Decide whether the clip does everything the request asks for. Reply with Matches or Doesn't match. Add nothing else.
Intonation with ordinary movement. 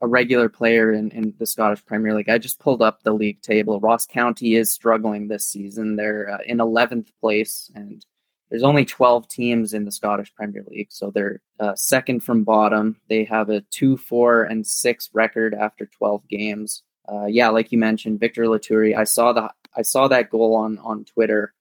Doesn't match